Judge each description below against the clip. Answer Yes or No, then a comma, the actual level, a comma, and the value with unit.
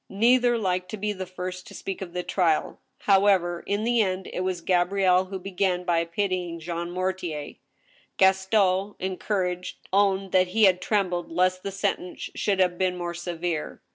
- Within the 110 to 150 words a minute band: No, average, 170 wpm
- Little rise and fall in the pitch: Yes, narrow, 1.7 semitones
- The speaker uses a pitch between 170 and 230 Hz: Yes, medium, 185 Hz